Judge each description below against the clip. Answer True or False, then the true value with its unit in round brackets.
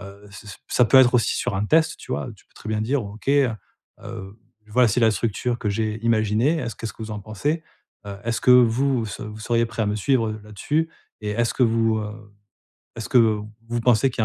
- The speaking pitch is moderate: False (115 Hz)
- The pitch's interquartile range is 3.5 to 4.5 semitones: False (2.7 semitones)